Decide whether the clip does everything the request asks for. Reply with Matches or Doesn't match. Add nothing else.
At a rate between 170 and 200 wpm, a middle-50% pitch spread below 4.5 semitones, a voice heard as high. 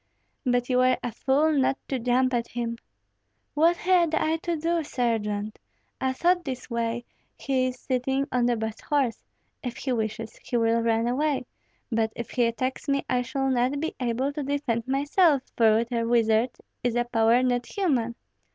Matches